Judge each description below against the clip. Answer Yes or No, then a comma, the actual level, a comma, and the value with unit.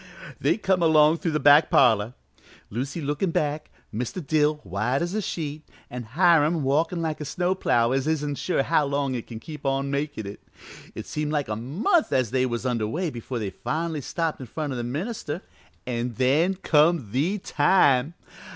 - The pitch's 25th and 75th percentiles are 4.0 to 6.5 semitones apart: Yes, average, 4.5 semitones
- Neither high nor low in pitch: Yes, medium, 145 Hz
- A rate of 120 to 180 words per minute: No, average, 190 wpm